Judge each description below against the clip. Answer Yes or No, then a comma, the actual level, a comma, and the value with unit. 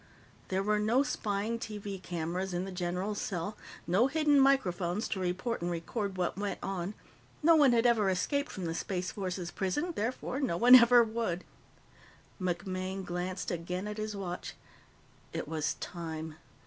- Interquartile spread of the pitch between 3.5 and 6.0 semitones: Yes, average, 4.3 semitones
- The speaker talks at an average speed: Yes, average, 160 wpm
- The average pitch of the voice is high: Yes, high, 195 Hz